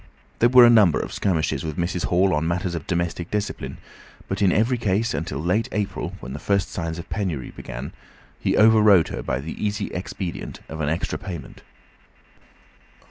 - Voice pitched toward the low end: Yes, very low, 90 Hz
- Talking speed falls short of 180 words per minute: No, average, 185 wpm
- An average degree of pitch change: Yes, average, 4.2 semitones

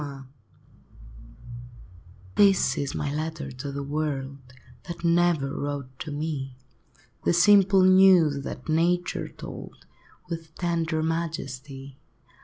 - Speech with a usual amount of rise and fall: Yes, average, 3.6 semitones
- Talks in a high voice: No, medium, 155 Hz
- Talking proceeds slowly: Yes, slow, 105 wpm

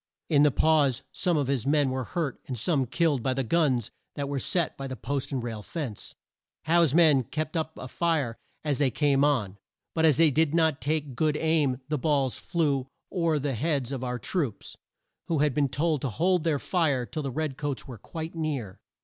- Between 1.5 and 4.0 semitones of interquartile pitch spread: Yes, average, 3.5 semitones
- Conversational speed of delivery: No, fast, 210 wpm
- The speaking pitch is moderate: Yes, medium, 145 Hz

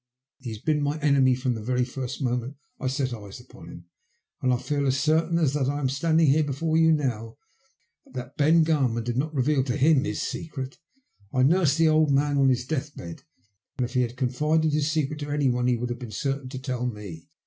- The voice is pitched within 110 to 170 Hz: Yes, low, 135 Hz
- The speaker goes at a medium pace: No, fast, 225 wpm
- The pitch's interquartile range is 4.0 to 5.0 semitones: No, average, 3.3 semitones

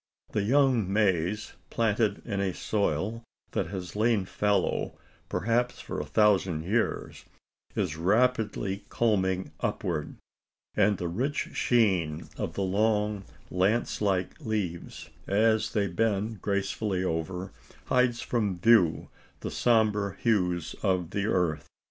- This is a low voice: Yes, low, 100 Hz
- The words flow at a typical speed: No, slow, 120 wpm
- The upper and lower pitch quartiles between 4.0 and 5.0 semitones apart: No, average, 3.3 semitones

